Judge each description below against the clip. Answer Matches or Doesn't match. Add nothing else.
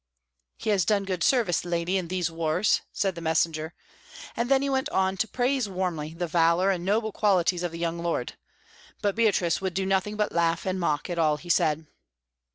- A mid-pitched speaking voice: Matches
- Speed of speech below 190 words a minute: Doesn't match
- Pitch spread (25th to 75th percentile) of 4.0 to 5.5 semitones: Doesn't match